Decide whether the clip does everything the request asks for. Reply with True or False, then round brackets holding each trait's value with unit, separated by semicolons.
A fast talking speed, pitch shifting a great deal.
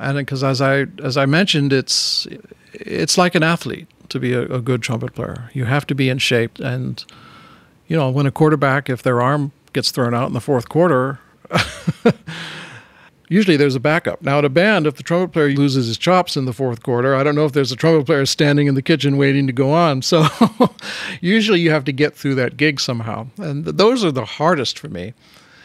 False (220 wpm; 3.5 semitones)